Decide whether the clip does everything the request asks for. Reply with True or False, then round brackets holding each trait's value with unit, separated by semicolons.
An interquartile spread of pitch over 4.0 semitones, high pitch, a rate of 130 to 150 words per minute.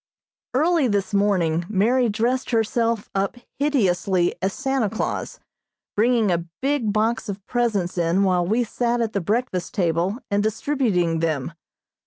True (4.7 semitones; 210 Hz; 140 wpm)